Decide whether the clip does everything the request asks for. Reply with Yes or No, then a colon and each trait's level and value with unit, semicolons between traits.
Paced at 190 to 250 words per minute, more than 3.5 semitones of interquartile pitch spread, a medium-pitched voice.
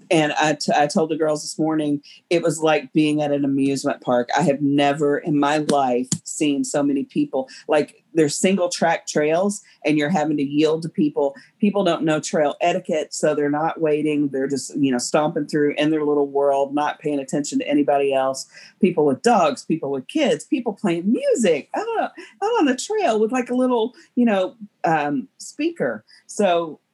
Yes: average, 195 wpm; average, 5.3 semitones; medium, 155 Hz